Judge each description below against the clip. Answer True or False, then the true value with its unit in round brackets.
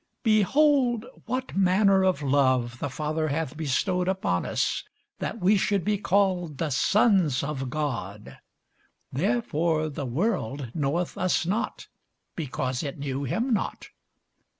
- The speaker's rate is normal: False (125 wpm)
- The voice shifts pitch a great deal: True (6.1 semitones)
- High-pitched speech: False (165 Hz)